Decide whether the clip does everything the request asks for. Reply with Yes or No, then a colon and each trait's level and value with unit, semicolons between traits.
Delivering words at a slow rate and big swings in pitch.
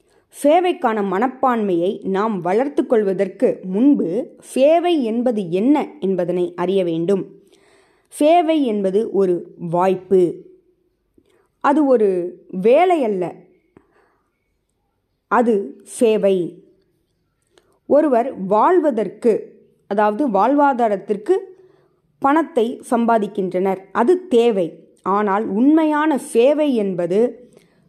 Yes: slow, 70 wpm; wide, 7.6 semitones